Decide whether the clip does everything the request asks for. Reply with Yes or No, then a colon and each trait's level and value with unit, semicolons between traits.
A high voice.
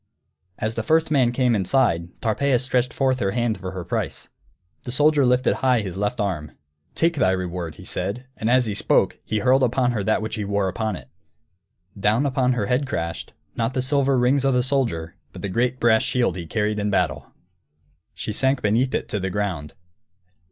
No: low, 115 Hz